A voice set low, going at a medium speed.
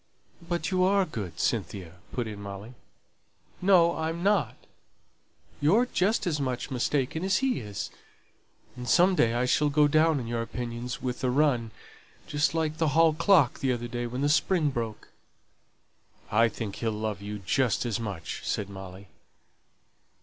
Yes: low, 125 Hz; average, 160 wpm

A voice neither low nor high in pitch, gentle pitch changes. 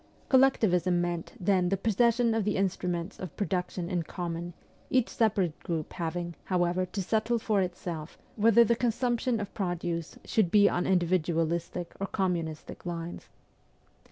No: medium, 180 Hz; average, 3.8 semitones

